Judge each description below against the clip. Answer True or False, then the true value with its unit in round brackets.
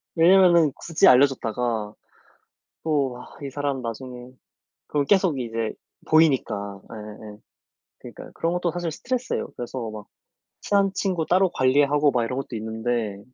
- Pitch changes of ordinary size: False (6.2 semitones)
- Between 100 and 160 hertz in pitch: True (135 Hz)